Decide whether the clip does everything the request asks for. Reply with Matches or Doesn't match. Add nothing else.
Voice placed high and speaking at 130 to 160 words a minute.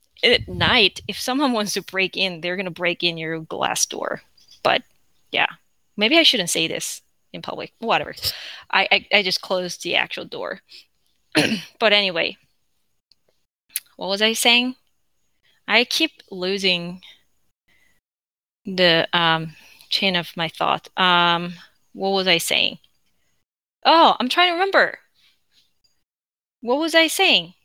Matches